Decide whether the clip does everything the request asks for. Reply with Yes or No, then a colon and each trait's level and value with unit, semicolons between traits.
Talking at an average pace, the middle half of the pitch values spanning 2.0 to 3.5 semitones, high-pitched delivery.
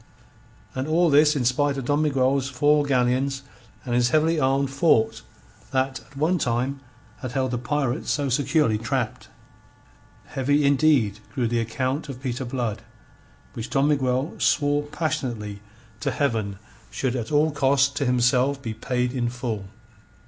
No: average, 150 wpm; average, 2.8 semitones; low, 135 Hz